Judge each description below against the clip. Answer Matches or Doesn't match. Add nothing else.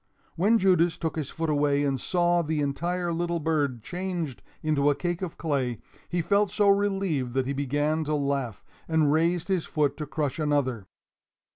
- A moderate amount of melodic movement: Matches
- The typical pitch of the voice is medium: Matches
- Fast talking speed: Doesn't match